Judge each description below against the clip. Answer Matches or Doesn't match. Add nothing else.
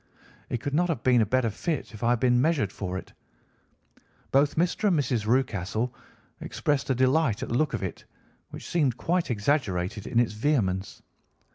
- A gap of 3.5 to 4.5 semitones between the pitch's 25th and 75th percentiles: Doesn't match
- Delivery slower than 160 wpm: Doesn't match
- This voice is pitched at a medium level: Doesn't match